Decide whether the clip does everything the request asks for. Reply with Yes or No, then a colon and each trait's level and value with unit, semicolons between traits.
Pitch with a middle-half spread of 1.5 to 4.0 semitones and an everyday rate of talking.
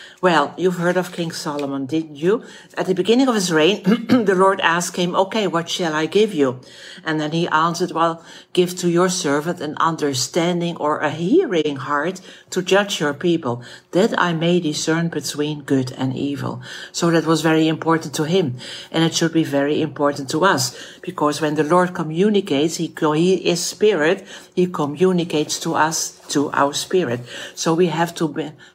Yes: average, 3.1 semitones; average, 180 wpm